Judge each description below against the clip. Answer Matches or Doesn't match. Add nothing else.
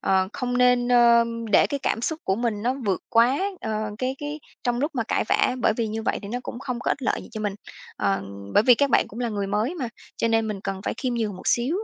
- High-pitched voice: Matches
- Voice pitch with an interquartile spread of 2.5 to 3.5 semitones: Matches